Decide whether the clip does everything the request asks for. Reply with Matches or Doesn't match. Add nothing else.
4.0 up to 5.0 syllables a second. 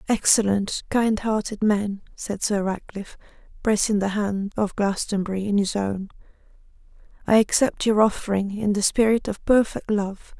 Matches